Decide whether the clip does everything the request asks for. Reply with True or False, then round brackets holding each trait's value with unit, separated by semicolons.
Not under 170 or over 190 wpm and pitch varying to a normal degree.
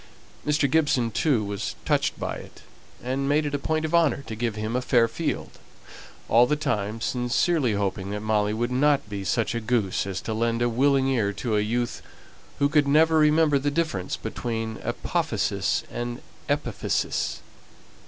True (175 wpm; 4.8 semitones)